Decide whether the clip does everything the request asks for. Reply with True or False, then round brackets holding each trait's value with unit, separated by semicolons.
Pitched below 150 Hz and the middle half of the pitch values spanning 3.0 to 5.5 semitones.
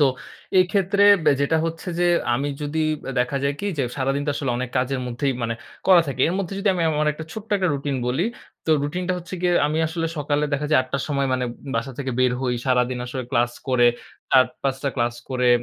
True (140 Hz; 4.2 semitones)